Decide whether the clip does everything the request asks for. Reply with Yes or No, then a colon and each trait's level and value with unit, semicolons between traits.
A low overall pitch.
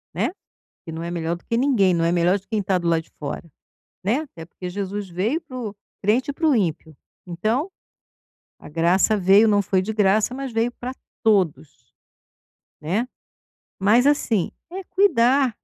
No: high, 205 Hz